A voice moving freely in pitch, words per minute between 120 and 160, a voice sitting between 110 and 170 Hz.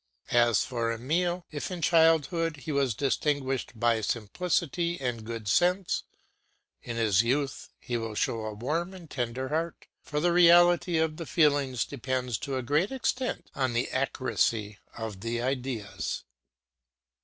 Yes: wide, 5.9 semitones; average, 145 wpm; low, 135 Hz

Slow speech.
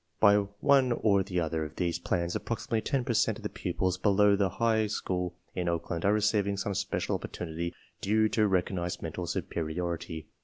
No: average, 185 wpm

